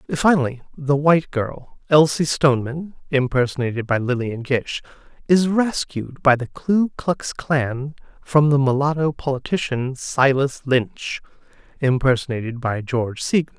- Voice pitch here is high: No, medium, 140 Hz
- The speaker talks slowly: Yes, slow, 120 wpm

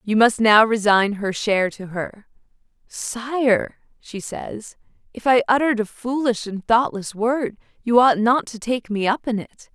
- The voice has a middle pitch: No, high, 225 Hz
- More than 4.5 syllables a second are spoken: No, 4.2 syllables/s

